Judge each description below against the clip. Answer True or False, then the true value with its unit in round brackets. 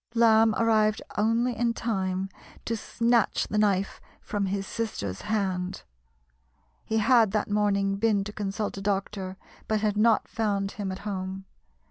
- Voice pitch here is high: True (210 Hz)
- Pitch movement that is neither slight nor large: False (2.2 semitones)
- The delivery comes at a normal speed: True (145 wpm)